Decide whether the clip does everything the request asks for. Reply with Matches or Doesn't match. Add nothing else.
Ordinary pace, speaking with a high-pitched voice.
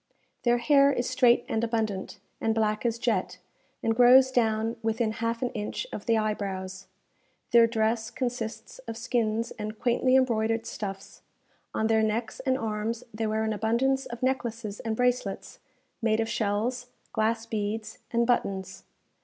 Matches